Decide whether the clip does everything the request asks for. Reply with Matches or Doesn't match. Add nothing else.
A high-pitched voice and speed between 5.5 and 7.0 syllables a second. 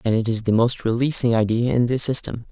Doesn't match